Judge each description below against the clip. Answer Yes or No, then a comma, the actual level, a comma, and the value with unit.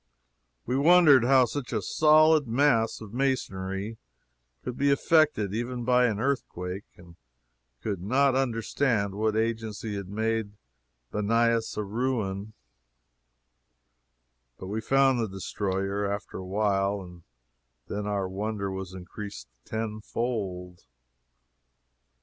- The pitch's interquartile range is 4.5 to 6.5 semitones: No, average, 4.1 semitones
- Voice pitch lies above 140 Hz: No, low, 110 Hz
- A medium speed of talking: No, slow, 115 wpm